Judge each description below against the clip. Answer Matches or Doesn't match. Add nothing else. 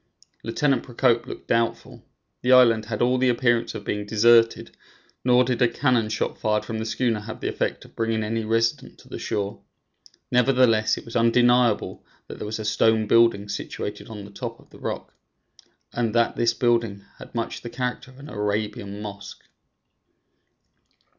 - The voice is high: Doesn't match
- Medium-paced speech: Matches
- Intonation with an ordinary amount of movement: Doesn't match